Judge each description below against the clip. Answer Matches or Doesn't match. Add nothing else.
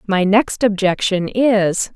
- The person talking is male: Doesn't match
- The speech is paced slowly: Matches